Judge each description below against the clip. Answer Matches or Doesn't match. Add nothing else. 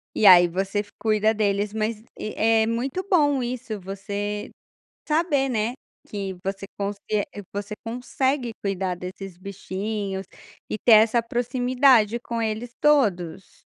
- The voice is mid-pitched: Doesn't match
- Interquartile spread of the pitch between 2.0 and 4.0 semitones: Matches